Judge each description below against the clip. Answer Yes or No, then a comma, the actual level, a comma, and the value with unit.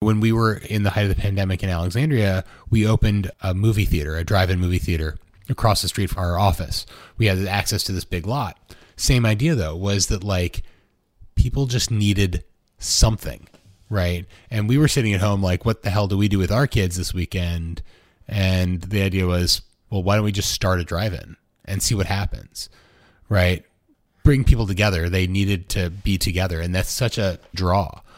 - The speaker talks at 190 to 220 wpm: Yes, average, 200 wpm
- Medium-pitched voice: No, very low, 95 Hz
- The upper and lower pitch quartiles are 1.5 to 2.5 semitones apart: No, average, 2.9 semitones